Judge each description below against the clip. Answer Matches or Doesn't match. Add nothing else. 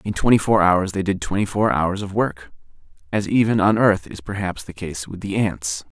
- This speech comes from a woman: Doesn't match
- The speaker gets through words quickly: Matches